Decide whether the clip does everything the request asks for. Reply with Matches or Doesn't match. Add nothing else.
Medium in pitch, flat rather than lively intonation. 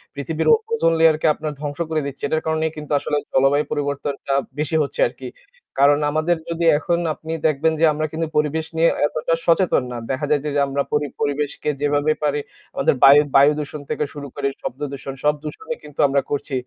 Matches